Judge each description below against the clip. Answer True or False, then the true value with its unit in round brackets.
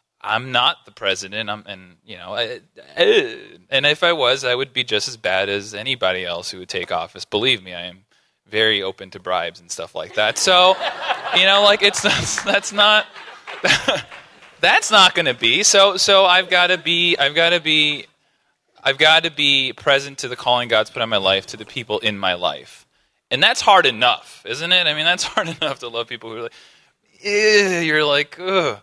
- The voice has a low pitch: False (145 Hz)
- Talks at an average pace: False (210 wpm)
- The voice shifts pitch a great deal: True (8.9 semitones)